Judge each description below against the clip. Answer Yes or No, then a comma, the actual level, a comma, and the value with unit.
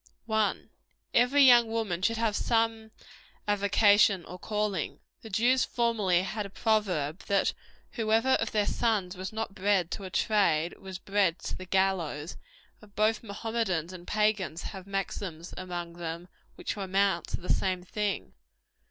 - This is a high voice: Yes, high, 200 Hz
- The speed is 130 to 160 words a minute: Yes, average, 150 wpm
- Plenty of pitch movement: No, average, 3.3 semitones